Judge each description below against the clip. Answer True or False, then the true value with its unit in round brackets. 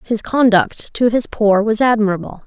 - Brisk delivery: False (170 wpm)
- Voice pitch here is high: True (220 Hz)